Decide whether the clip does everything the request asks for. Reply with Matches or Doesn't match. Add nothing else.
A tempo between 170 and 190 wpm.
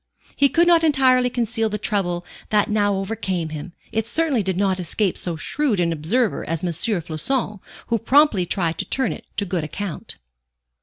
Matches